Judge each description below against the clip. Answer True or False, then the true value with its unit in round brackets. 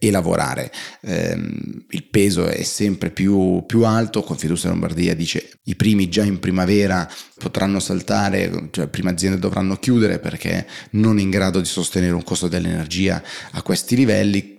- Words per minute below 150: False (165 wpm)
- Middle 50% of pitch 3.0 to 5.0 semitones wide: False (2.6 semitones)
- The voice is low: True (95 Hz)